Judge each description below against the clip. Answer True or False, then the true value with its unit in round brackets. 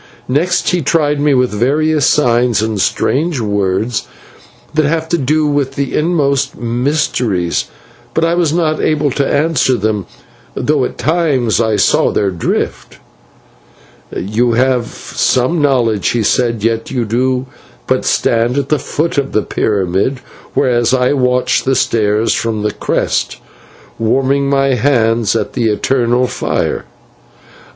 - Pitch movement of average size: True (4.1 semitones)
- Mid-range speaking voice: False (125 Hz)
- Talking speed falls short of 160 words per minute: True (140 wpm)